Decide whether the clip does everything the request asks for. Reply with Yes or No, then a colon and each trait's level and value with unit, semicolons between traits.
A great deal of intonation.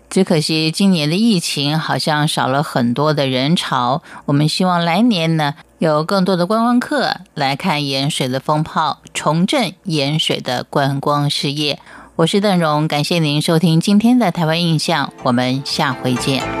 No: average, 3.8 semitones